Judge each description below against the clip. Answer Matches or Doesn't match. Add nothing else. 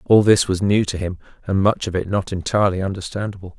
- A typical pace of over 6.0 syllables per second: Matches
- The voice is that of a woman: Doesn't match